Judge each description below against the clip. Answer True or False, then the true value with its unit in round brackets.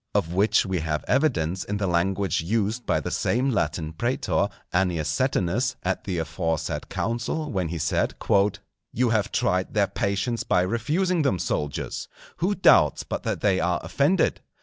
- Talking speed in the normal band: True (155 wpm)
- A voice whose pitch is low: True (95 Hz)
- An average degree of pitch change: False (5.9 semitones)